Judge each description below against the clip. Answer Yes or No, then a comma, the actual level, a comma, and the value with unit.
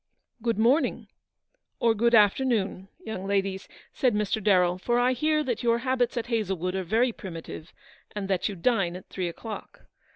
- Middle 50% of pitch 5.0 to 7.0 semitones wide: No, average, 4.0 semitones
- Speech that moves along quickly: No, average, 170 wpm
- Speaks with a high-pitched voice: Yes, high, 215 Hz